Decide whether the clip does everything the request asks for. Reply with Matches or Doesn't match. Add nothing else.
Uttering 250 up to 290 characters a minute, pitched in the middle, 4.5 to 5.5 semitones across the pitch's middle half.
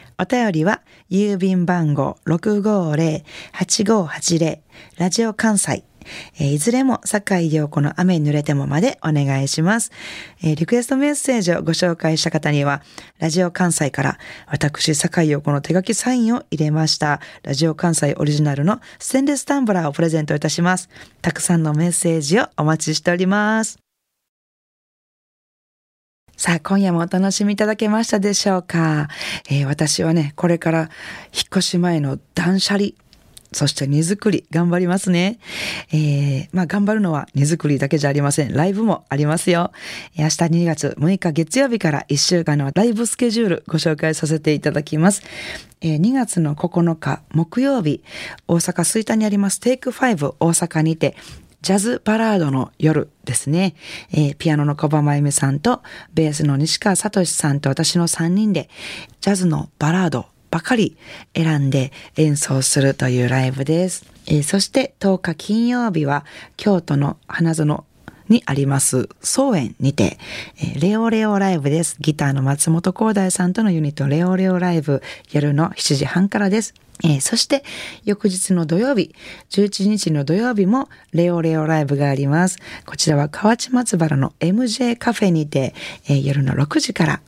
Matches